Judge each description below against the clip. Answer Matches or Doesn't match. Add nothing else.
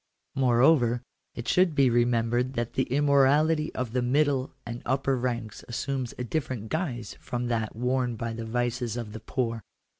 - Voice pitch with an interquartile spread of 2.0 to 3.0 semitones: Matches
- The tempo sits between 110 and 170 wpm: Matches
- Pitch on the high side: Doesn't match